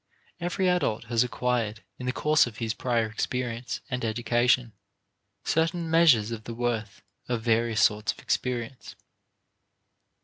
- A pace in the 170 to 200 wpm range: No, slow, 135 wpm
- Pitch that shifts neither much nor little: No, narrow, 2.0 semitones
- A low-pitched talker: Yes, low, 120 Hz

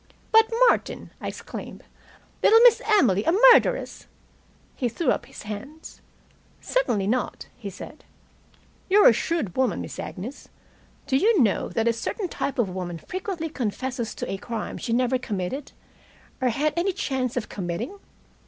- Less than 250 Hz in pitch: No, very high, 255 Hz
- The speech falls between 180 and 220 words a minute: No, average, 155 wpm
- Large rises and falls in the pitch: Yes, wide, 8.0 semitones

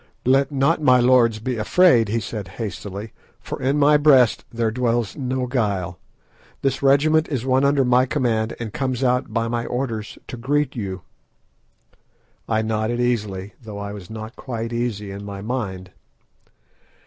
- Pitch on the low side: Yes, low, 120 Hz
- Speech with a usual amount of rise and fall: Yes, average, 3.4 semitones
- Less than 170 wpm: Yes, average, 160 wpm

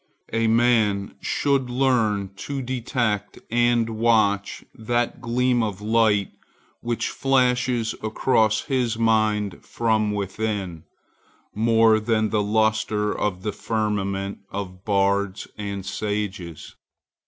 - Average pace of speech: No, slow, 105 wpm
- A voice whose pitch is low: Yes, low, 110 Hz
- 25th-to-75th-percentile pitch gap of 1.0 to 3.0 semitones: Yes, narrow, 2.6 semitones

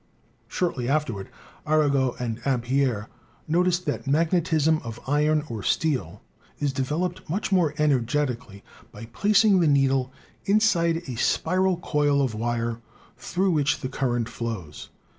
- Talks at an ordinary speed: No, slow, 130 wpm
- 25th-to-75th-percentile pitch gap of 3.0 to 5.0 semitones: No, wide, 5.5 semitones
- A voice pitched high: No, medium, 140 Hz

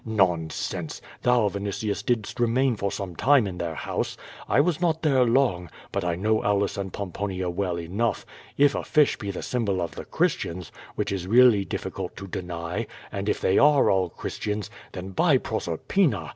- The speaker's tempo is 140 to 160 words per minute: No, average, 185 wpm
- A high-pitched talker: No, low, 100 Hz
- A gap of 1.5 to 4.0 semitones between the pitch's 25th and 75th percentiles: No, average, 5.1 semitones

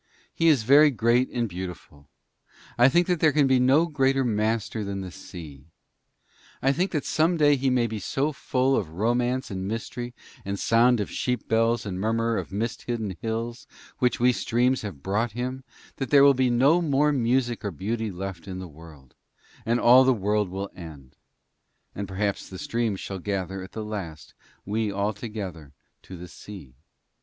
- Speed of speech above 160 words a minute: Yes, average, 185 wpm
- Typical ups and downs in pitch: Yes, average, 4.8 semitones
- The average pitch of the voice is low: Yes, low, 115 Hz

